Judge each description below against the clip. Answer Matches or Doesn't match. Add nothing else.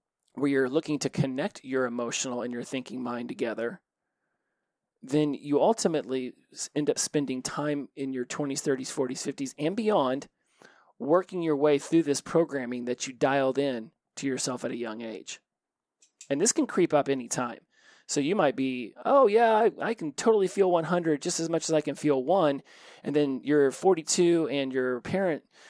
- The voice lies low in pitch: Doesn't match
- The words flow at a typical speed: Matches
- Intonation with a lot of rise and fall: Doesn't match